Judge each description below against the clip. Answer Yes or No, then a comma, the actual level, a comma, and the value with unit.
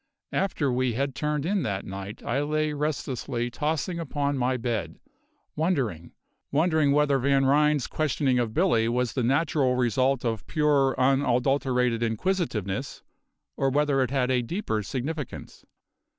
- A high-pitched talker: No, low, 135 Hz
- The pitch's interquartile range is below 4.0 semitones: Yes, average, 3.5 semitones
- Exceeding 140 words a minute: No, slow, 135 wpm